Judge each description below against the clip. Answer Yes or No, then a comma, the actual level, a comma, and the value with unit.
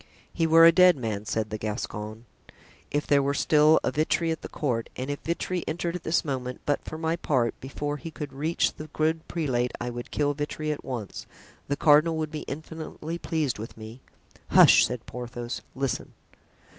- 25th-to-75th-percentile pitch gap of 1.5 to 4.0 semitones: No, average, 4.6 semitones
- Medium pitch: Yes, medium, 145 Hz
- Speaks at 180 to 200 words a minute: Yes, average, 190 wpm